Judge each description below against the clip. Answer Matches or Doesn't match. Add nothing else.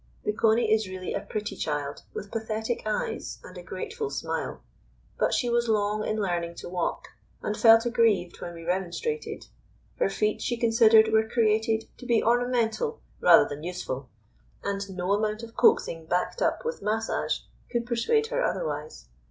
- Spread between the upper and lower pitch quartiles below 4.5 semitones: Matches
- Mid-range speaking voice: Doesn't match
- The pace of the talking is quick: Doesn't match